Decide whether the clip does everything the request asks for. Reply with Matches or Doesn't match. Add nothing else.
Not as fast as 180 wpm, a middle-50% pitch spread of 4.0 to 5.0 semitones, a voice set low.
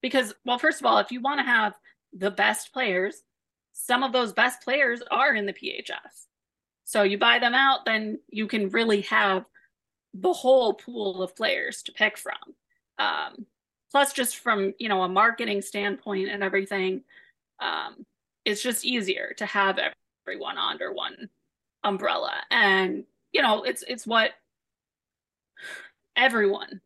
Doesn't match